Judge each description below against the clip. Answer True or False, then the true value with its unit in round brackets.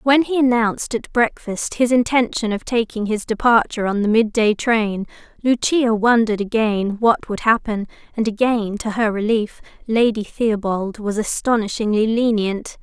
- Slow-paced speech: False (145 wpm)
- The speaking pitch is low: False (225 Hz)